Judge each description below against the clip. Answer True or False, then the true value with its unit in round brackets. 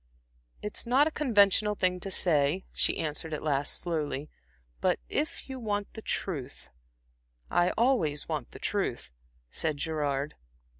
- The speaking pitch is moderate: True (170 Hz)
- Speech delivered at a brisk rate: False (140 wpm)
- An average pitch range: False (5.9 semitones)